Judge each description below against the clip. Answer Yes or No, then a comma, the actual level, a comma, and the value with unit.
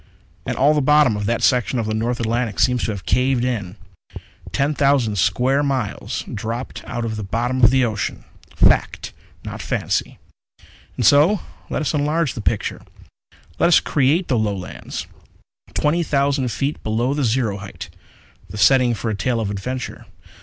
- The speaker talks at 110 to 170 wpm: Yes, average, 165 wpm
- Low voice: Yes, low, 125 Hz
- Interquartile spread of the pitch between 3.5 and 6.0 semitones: Yes, average, 4.0 semitones